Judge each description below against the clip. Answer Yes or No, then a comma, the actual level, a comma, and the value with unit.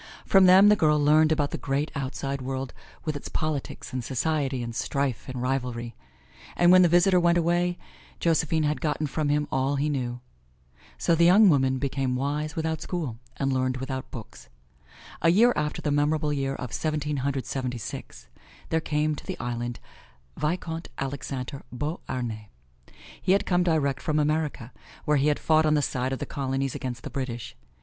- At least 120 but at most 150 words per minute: No, average, 180 wpm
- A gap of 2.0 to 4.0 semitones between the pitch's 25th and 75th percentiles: Yes, average, 3.3 semitones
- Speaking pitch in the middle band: Yes, medium, 145 Hz